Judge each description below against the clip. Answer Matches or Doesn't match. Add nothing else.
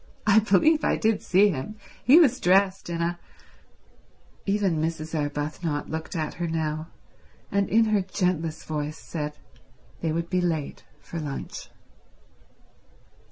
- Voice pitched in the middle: Matches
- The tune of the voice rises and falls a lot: Doesn't match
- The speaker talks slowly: Matches